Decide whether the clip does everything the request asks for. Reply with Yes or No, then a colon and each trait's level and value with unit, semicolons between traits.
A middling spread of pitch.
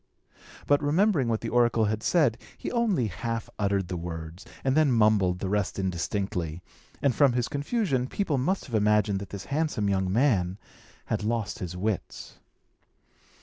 No: wide, 6.2 semitones